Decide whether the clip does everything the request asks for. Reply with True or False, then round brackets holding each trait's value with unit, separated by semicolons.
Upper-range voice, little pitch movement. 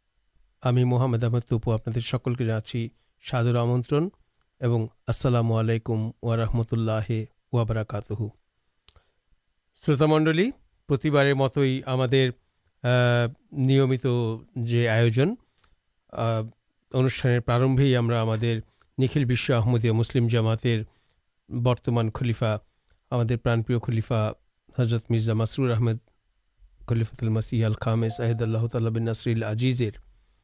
False (120 Hz; 1.9 semitones)